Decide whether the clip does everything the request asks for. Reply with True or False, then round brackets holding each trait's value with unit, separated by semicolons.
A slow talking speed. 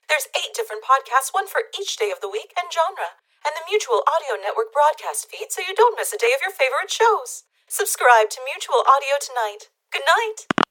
False (205 wpm)